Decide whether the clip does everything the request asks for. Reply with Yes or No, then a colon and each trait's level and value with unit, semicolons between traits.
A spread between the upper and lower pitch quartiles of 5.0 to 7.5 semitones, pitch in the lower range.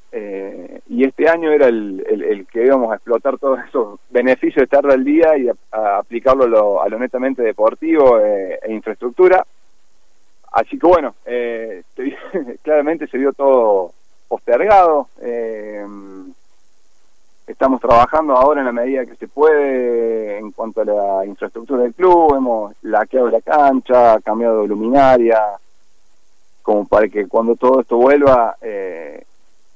Yes: wide, 5.4 semitones; low, 125 Hz